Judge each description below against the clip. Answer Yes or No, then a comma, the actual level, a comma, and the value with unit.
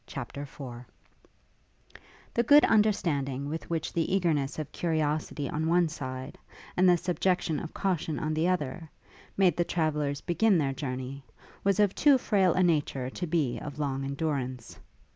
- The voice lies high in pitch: No, medium, 155 Hz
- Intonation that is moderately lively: Yes, average, 4.3 semitones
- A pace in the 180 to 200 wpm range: No, average, 155 wpm